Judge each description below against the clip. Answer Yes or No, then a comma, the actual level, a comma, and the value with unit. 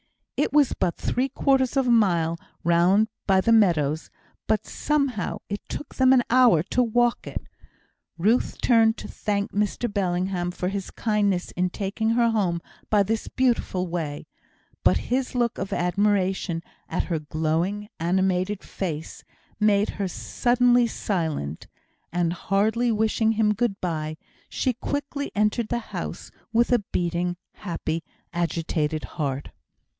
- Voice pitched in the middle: No, high, 200 Hz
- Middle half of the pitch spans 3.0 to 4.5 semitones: No, average, 5.0 semitones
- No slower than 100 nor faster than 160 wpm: Yes, average, 140 wpm